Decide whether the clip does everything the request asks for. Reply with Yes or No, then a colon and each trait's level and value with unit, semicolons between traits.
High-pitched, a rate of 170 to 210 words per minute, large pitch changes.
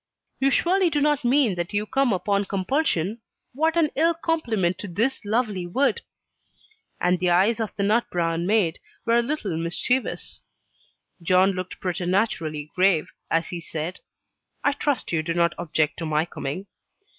No: high, 195 Hz; average, 160 wpm; wide, 6.8 semitones